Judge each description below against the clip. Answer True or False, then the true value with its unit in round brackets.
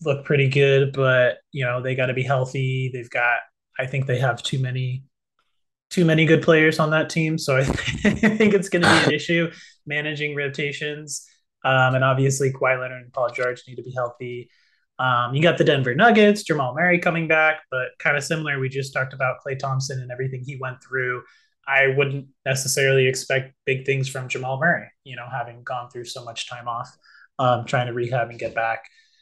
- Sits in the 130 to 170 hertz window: True (135 Hz)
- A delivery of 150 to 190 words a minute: False (205 wpm)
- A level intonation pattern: False (3.3 semitones)